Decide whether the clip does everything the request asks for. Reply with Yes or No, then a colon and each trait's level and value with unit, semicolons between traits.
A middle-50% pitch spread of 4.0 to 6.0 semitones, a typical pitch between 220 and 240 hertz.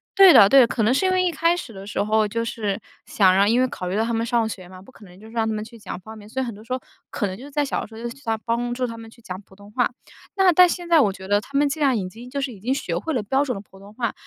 Yes: average, 4.4 semitones; high, 230 Hz